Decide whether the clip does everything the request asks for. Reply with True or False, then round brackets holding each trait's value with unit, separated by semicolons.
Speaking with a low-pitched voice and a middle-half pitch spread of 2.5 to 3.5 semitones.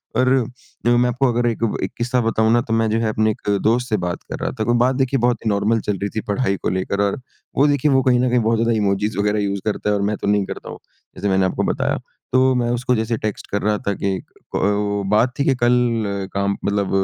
True (110 Hz; 3.2 semitones)